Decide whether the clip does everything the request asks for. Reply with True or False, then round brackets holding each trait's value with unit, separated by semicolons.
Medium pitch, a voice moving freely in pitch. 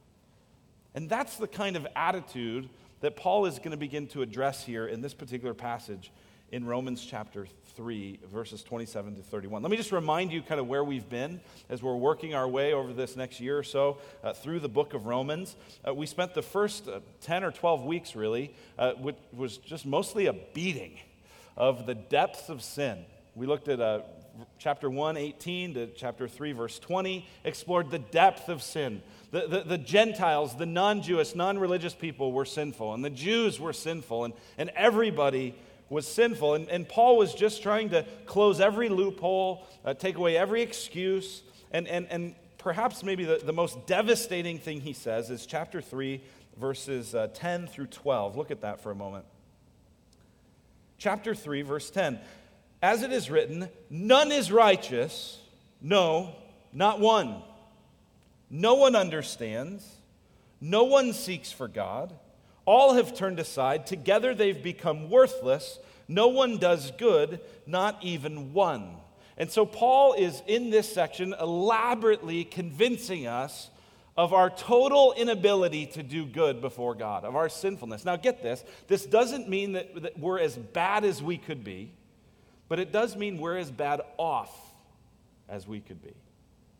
True (165 Hz; 7.0 semitones)